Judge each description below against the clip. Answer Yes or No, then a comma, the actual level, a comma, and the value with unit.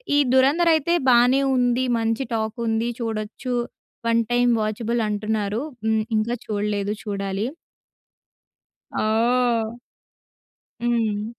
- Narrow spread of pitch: Yes, narrow, 2.2 semitones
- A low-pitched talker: No, high, 225 Hz